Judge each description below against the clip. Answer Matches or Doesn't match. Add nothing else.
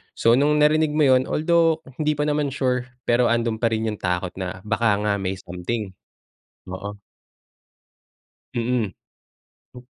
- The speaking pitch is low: Matches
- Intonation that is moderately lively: Doesn't match